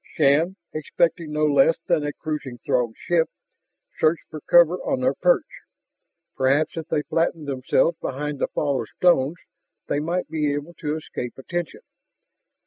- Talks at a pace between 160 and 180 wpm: No, average, 150 wpm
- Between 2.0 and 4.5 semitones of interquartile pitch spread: Yes, average, 3.0 semitones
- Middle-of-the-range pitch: Yes, medium, 155 Hz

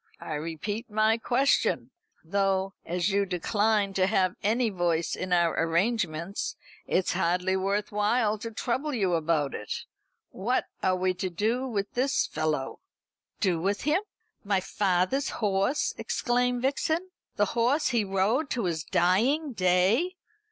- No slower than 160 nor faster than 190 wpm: No, average, 140 wpm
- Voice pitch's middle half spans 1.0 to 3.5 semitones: No, average, 4.6 semitones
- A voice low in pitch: No, high, 200 Hz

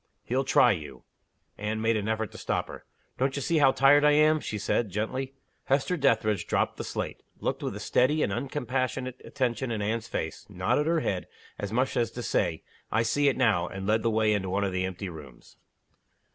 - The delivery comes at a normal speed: No, fast, 210 wpm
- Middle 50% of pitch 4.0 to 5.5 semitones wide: Yes, average, 4.6 semitones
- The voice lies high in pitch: No, low, 115 Hz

